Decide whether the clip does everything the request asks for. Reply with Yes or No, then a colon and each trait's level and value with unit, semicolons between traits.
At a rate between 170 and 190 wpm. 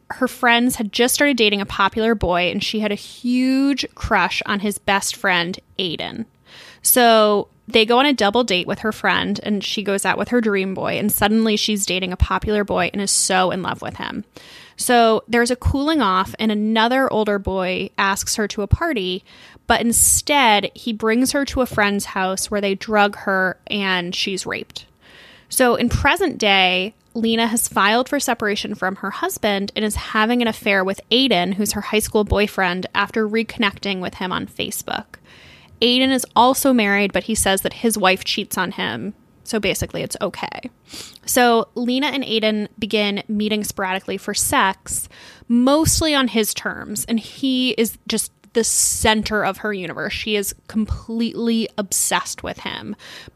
Yes: average, 175 wpm